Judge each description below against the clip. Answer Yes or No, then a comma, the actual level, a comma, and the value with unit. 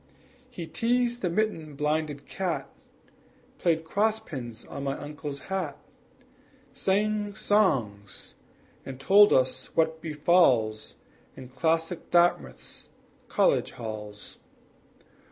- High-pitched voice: No, medium, 160 Hz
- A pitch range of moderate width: No, wide, 6.5 semitones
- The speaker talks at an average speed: No, slow, 100 wpm